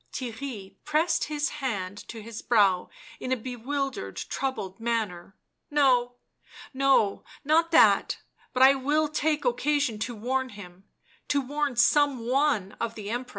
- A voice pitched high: Yes, very high, 255 Hz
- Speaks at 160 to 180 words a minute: No, average, 150 wpm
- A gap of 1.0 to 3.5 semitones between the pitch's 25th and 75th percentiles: No, average, 4.8 semitones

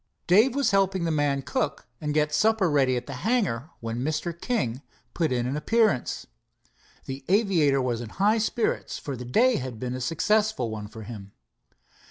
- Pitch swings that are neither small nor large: No, wide, 8.0 semitones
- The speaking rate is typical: Yes, average, 175 wpm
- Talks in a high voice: No, medium, 150 Hz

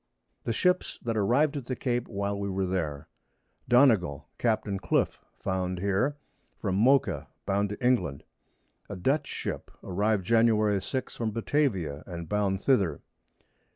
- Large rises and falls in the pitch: No, average, 4.6 semitones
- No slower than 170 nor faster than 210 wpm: No, average, 140 wpm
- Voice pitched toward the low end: Yes, low, 105 Hz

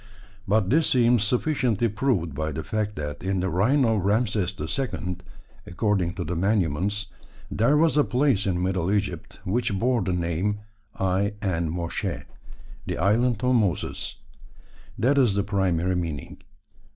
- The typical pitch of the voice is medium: No, low, 100 Hz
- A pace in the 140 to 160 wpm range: Yes, average, 150 wpm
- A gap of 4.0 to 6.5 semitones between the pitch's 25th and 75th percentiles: Yes, average, 4.7 semitones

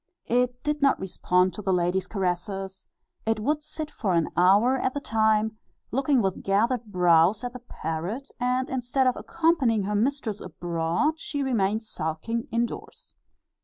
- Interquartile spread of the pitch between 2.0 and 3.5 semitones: No, average, 5.3 semitones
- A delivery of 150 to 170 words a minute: Yes, average, 160 wpm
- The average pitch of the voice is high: Yes, high, 220 Hz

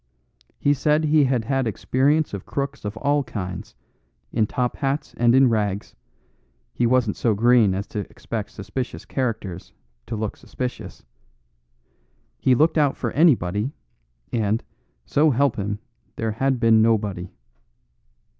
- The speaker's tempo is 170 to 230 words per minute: No, slow, 135 wpm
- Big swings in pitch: No, average, 4.5 semitones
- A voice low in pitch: Yes, low, 120 Hz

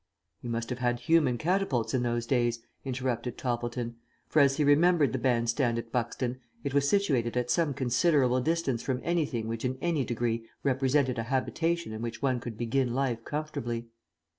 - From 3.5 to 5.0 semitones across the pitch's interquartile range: No, average, 3.1 semitones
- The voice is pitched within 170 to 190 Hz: No, low, 125 Hz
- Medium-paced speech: Yes, average, 180 wpm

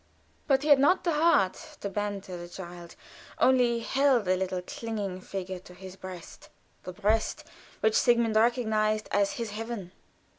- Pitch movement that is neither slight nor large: Yes, average, 4.2 semitones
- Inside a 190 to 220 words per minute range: No, average, 155 wpm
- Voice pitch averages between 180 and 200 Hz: No, high, 210 Hz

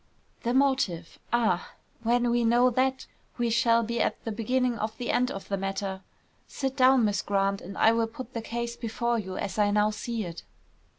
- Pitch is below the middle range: No, high, 230 Hz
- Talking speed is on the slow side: No, average, 195 wpm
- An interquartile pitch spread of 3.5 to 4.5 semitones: No, average, 2.9 semitones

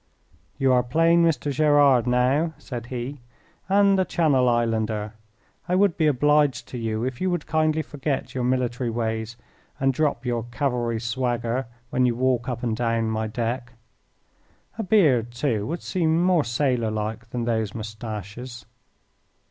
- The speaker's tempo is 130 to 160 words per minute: Yes, average, 155 wpm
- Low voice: Yes, low, 125 Hz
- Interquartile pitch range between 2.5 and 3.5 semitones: No, average, 4.1 semitones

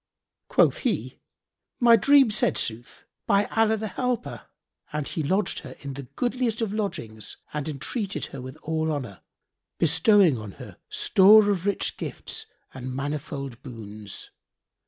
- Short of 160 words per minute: Yes, average, 140 wpm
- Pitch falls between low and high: Yes, medium, 160 Hz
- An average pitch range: No, wide, 8.5 semitones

